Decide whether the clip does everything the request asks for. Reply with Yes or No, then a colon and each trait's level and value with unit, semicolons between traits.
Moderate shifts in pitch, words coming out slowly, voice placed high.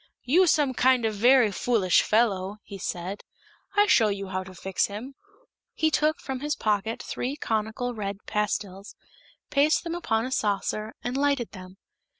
No: average, 4.8 semitones; average, 160 wpm; high, 220 Hz